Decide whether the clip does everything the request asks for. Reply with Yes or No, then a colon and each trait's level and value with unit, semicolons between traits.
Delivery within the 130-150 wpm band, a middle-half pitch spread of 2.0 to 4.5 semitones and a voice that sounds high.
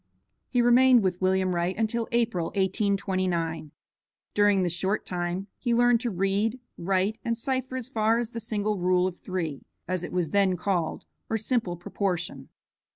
No: average, 160 wpm; average, 4.1 semitones; high, 195 Hz